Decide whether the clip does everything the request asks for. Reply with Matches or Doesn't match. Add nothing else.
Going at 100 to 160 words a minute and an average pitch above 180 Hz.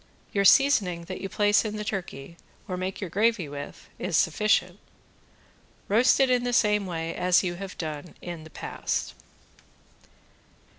Matches